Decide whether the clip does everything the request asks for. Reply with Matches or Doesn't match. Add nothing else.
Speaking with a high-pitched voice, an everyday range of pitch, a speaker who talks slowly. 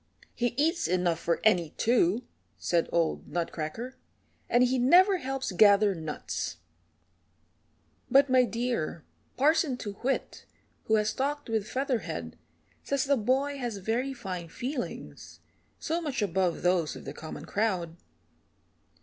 Doesn't match